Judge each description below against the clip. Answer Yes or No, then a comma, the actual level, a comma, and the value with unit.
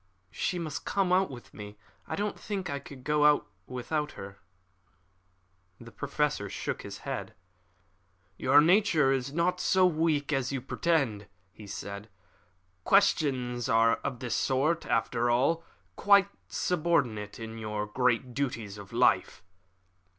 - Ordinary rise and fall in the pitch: No, wide, 6.2 semitones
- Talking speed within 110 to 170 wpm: Yes, slow, 135 wpm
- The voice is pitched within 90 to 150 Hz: Yes, low, 135 Hz